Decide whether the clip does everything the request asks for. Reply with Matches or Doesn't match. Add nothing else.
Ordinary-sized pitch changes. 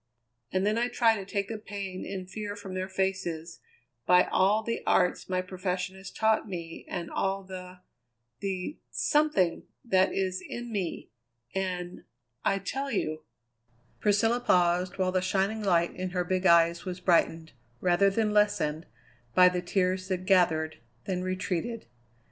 Doesn't match